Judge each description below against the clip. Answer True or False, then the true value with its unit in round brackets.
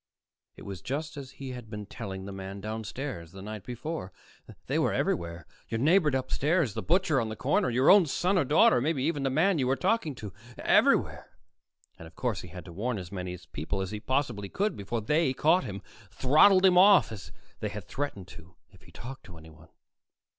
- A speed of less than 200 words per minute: False (205 wpm)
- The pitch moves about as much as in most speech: False (7.4 semitones)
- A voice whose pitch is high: False (125 Hz)